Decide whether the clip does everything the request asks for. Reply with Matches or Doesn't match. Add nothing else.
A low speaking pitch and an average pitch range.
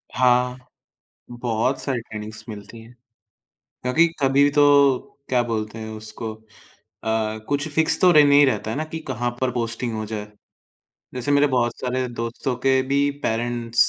Matches